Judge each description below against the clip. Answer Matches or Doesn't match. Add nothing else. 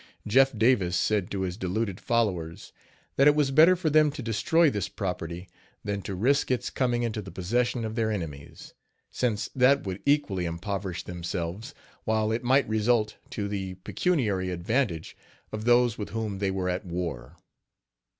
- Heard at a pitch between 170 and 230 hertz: Doesn't match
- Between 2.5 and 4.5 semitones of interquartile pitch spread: Doesn't match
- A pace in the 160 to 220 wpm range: Matches